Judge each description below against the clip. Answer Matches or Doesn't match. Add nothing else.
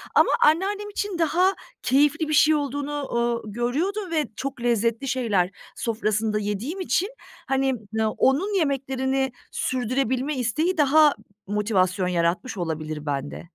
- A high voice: Matches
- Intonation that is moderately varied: Doesn't match